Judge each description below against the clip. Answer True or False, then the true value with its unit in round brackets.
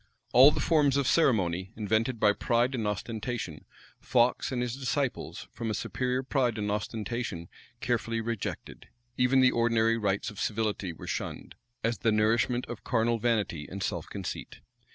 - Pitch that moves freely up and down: False (2.8 semitones)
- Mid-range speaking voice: False (115 Hz)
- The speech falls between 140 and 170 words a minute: True (155 wpm)